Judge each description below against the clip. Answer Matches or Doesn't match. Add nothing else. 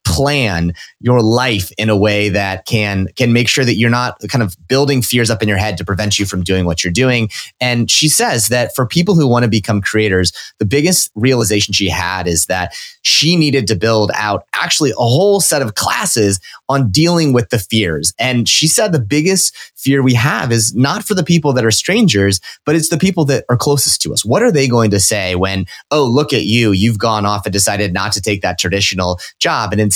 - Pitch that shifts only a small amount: Doesn't match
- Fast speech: Matches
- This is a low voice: Matches